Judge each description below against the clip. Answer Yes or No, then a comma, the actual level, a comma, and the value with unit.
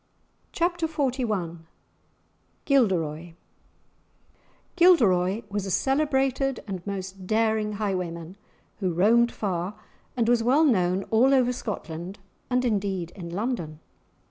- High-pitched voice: Yes, high, 210 Hz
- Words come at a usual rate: No, slow, 105 wpm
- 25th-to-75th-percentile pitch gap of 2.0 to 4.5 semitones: No, wide, 5.6 semitones